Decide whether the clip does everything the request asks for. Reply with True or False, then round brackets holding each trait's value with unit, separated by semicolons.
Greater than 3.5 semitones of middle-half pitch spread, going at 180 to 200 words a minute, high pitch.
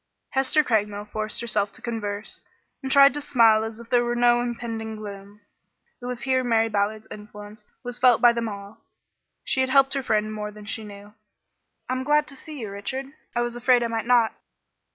False (2.9 semitones; 195 wpm; 230 Hz)